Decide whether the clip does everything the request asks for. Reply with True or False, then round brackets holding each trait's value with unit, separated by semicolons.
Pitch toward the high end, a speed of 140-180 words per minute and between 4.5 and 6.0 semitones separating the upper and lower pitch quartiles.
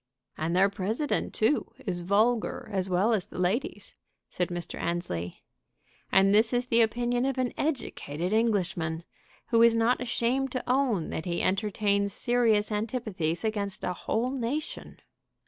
True (215 Hz; 145 wpm; 4.8 semitones)